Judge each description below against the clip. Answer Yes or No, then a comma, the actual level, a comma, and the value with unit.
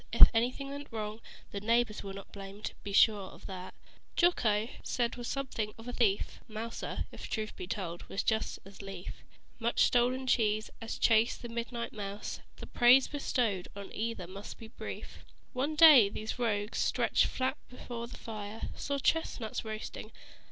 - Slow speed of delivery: No, average, 170 wpm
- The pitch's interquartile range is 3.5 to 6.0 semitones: No, average, 3.0 semitones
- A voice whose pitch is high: Yes, high, 225 Hz